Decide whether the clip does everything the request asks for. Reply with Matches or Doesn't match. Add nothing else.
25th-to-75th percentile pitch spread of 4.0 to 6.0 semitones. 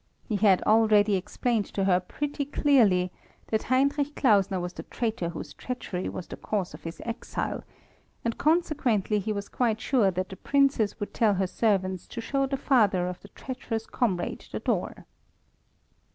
Matches